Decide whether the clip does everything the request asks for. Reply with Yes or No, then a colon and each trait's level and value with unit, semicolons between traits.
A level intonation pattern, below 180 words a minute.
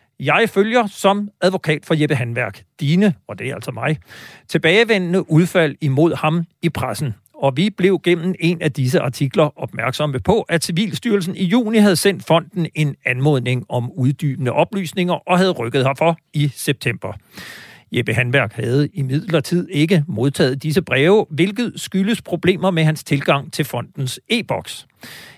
No: average, 5.0 semitones; average, 155 wpm